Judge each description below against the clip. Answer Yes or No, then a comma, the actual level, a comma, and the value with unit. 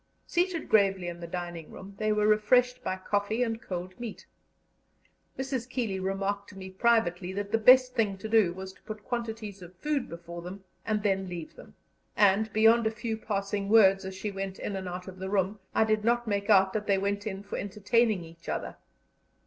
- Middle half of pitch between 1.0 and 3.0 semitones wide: Yes, average, 2.7 semitones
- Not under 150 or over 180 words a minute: No, fast, 205 wpm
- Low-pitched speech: No, high, 200 Hz